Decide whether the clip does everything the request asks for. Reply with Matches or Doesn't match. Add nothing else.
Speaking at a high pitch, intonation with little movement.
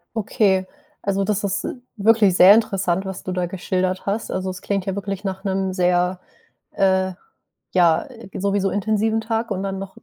Matches